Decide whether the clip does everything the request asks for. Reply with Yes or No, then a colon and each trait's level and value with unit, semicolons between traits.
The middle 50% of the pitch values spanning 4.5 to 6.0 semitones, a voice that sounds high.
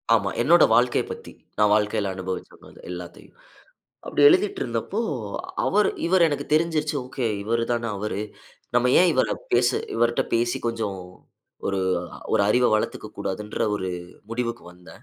No: wide, 5.6 semitones; low, 115 Hz